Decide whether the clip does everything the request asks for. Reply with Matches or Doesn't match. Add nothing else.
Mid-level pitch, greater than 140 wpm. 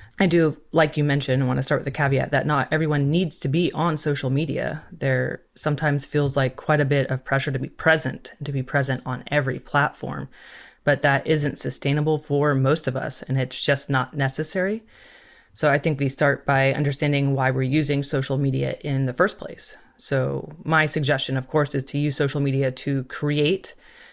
Matches